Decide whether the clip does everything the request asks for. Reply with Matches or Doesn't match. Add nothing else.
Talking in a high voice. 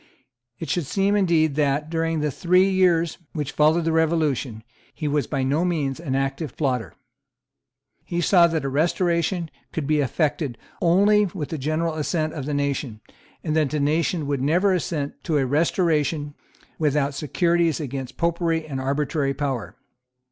Doesn't match